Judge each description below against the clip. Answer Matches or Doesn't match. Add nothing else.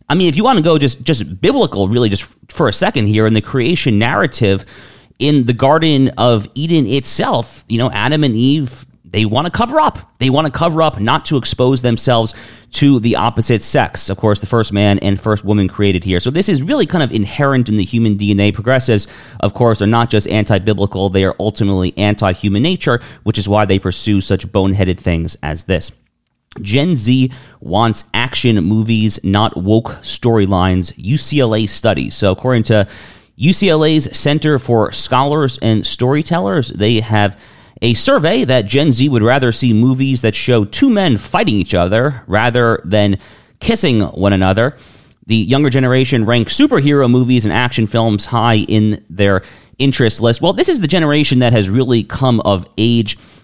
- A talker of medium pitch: Doesn't match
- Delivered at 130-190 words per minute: Matches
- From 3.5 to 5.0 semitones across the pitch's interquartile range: Matches